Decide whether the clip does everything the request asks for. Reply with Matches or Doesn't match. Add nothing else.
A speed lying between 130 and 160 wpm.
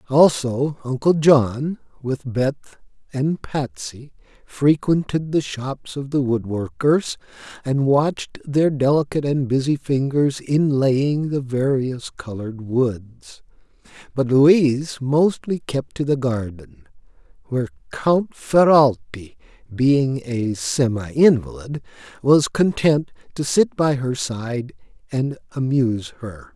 Doesn't match